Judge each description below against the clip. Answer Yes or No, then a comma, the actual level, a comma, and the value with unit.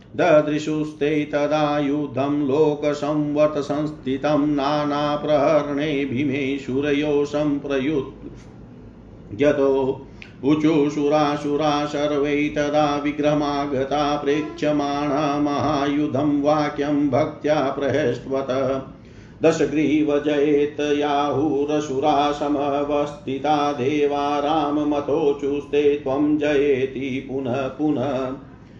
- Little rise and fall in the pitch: Yes, narrow, 1.1 semitones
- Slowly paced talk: Yes, slow, 45 wpm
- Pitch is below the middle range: No, medium, 145 Hz